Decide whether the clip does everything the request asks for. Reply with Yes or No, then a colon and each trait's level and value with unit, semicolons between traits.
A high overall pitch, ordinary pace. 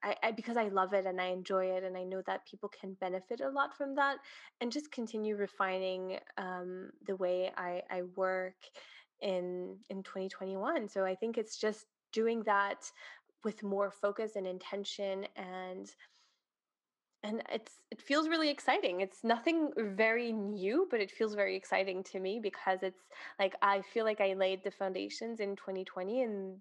Yes: high, 195 Hz; average, 180 wpm